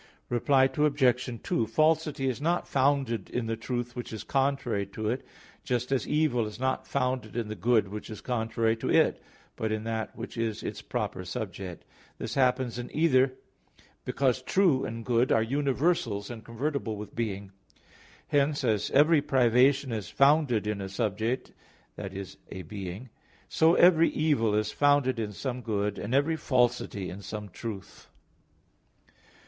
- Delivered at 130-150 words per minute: No, average, 160 wpm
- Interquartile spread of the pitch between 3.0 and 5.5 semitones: Yes, average, 4.1 semitones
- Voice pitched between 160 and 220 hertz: No, low, 120 Hz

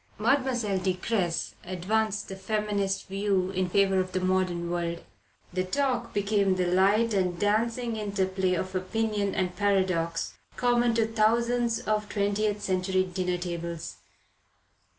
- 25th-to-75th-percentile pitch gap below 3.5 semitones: Yes, average, 2.7 semitones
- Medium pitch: No, high, 195 Hz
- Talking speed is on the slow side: Yes, slow, 130 wpm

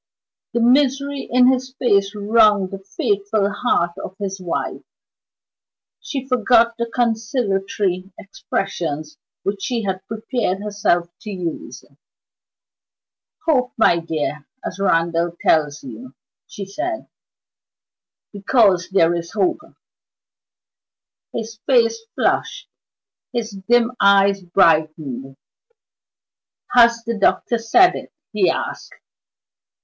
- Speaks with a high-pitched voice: Yes, high, 200 Hz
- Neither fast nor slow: No, slow, 105 wpm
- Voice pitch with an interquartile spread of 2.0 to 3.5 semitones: No, average, 4.6 semitones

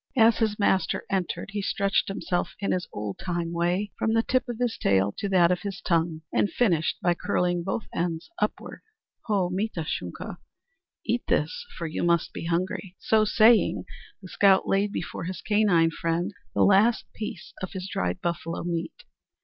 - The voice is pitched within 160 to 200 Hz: Yes, medium, 185 Hz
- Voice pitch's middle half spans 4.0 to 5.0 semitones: No, average, 3.4 semitones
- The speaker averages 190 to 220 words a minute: No, average, 175 wpm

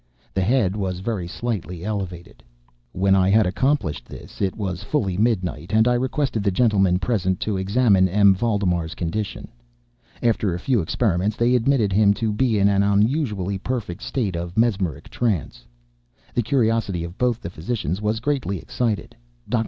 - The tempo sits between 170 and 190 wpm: No, average, 160 wpm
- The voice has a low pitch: Yes, low, 100 Hz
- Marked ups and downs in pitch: No, average, 4.1 semitones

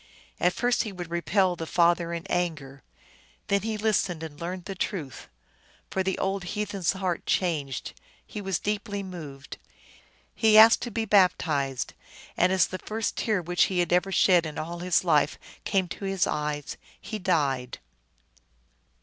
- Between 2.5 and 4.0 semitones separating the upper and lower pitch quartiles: Yes, average, 3.3 semitones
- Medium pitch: Yes, medium, 180 Hz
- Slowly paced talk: No, average, 165 wpm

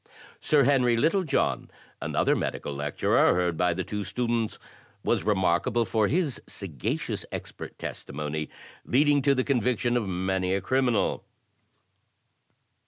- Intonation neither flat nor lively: No, wide, 6.0 semitones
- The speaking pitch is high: No, low, 110 Hz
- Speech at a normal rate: No, slow, 120 wpm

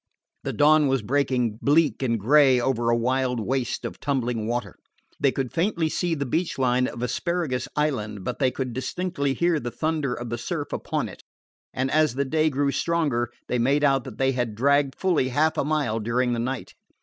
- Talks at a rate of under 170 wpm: No, average, 195 wpm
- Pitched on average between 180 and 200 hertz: No, low, 135 Hz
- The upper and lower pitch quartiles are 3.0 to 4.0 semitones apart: Yes, average, 3.6 semitones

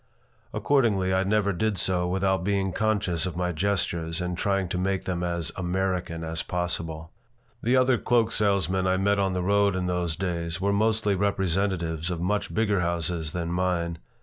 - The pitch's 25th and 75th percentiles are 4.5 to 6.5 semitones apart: No, narrow, 2.6 semitones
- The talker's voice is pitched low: Yes, very low, 95 Hz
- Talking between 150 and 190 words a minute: Yes, average, 175 wpm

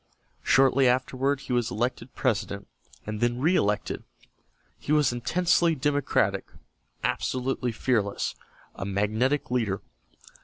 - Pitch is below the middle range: Yes, low, 125 Hz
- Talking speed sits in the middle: No, slow, 105 wpm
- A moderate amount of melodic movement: Yes, average, 3.8 semitones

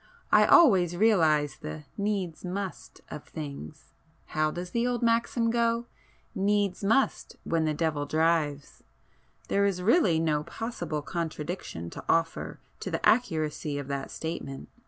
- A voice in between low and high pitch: Yes, medium, 170 Hz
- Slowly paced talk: Yes, slow, 130 wpm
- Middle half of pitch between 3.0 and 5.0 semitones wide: No, wide, 5.4 semitones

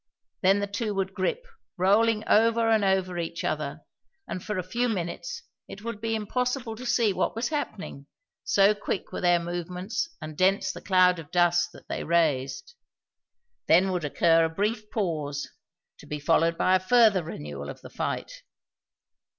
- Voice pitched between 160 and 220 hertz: Yes, medium, 185 Hz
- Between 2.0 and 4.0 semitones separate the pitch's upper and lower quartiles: No, average, 4.4 semitones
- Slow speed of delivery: No, average, 170 wpm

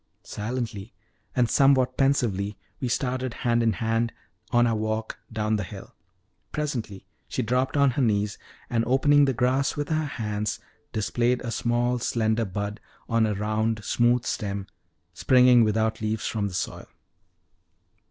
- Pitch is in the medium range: No, low, 115 Hz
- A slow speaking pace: No, average, 145 wpm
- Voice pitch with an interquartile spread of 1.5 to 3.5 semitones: Yes, average, 2.8 semitones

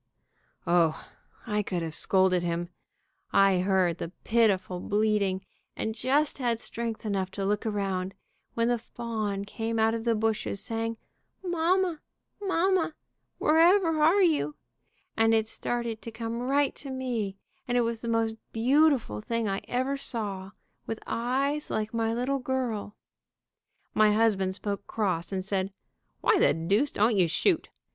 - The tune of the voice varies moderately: Yes, average, 4.3 semitones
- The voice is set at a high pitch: Yes, high, 225 Hz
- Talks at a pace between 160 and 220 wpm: No, average, 150 wpm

